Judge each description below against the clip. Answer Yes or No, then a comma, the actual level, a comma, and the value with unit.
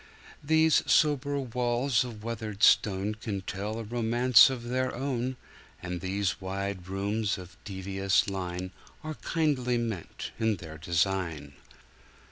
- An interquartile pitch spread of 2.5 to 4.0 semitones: No, average, 4.6 semitones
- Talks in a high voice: No, low, 110 Hz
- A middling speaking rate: No, slow, 120 wpm